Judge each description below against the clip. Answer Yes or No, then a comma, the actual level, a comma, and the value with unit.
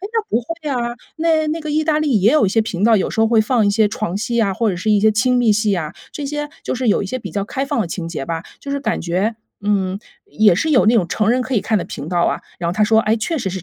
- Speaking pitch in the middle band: No, high, 220 Hz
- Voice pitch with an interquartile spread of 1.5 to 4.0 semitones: No, average, 4.7 semitones